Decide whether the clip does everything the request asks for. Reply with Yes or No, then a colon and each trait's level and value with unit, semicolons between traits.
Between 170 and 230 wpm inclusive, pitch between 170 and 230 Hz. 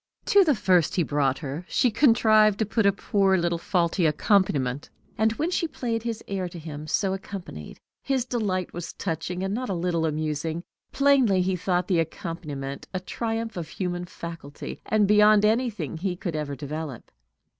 Yes: average, 175 wpm; medium, 185 Hz